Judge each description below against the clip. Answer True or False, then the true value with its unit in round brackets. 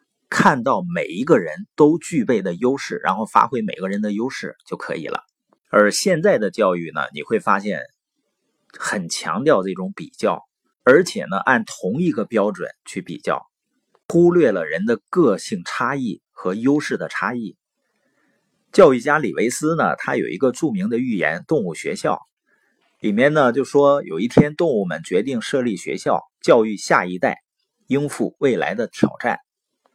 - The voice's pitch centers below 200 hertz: True (140 Hz)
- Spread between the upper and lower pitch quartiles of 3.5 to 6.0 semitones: False (7.3 semitones)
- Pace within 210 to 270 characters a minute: True (240 characters per minute)